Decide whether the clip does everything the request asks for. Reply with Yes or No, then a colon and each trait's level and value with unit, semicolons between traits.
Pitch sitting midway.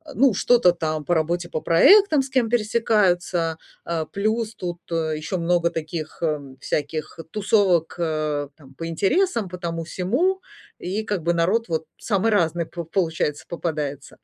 Yes: medium, 175 Hz